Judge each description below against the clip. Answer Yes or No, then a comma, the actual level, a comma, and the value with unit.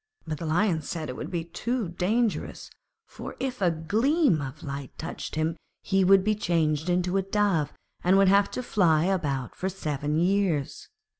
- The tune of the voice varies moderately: Yes, average, 4.1 semitones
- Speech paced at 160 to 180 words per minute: Yes, average, 175 wpm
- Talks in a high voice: No, medium, 180 Hz